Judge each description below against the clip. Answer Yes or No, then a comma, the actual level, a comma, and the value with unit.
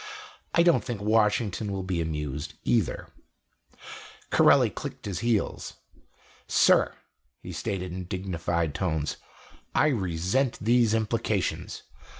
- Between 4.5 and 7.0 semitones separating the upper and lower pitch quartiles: Yes, average, 4.9 semitones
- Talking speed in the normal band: No, slow, 110 wpm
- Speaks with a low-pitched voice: Yes, very low, 95 Hz